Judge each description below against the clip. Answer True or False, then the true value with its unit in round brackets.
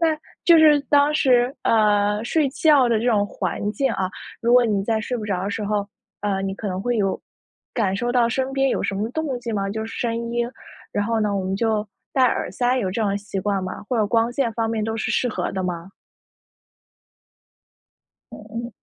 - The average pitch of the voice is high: True (225 Hz)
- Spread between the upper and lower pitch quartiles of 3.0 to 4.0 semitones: True (3.3 semitones)